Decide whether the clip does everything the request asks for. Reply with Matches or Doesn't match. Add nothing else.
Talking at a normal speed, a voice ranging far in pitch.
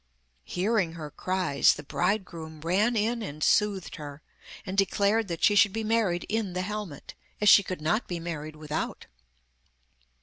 Doesn't match